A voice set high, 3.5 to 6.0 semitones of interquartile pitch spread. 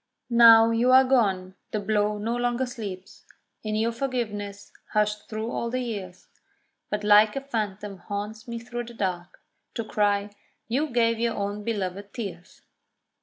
No: high, 215 Hz; narrow, 2.5 semitones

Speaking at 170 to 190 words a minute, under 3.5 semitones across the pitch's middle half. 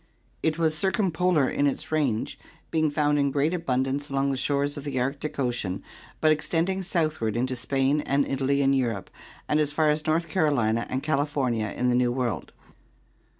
Yes: average, 180 wpm; average, 3.1 semitones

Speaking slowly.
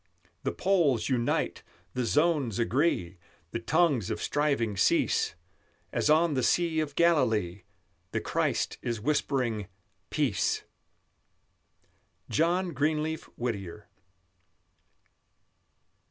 Yes: slow, 95 wpm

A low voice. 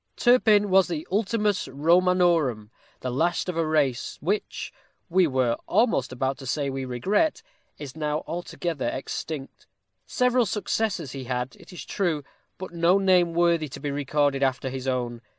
No: medium, 160 Hz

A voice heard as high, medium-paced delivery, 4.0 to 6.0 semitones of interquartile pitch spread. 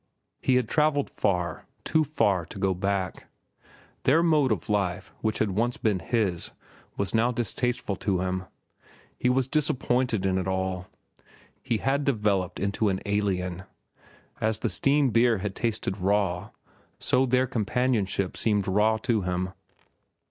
No: low, 105 Hz; average, 145 wpm; average, 4.8 semitones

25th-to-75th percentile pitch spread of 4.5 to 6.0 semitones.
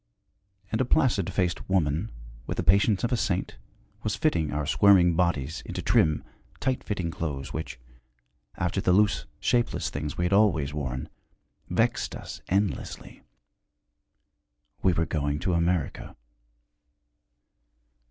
Yes: average, 4.9 semitones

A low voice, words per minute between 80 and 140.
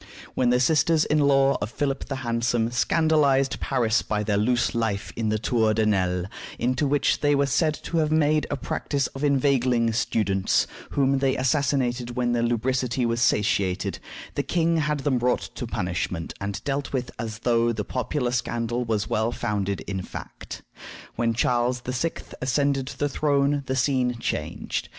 No: low, 125 Hz; average, 165 wpm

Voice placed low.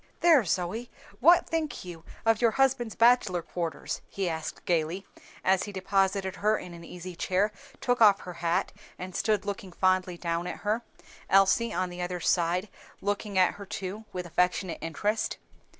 No: high, 190 Hz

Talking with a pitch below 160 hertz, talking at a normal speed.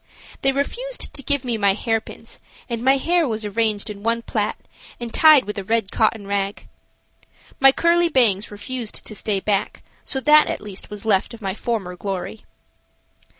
No: high, 225 Hz; average, 175 wpm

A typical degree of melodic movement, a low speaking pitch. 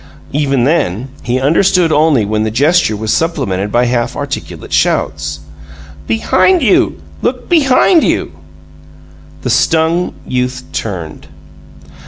No: wide, 7.2 semitones; low, 130 Hz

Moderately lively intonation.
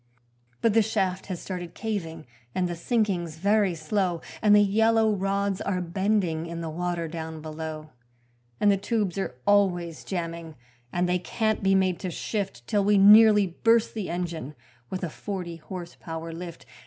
Yes: average, 3.5 semitones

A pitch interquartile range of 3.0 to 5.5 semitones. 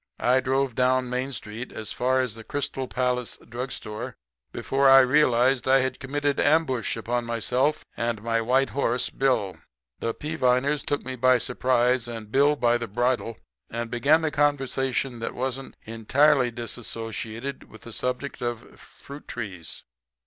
No: narrow, 2.4 semitones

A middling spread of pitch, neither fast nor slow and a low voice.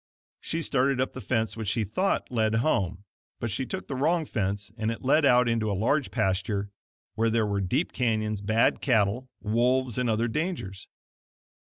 Yes: average, 3.6 semitones; average, 180 wpm; low, 115 Hz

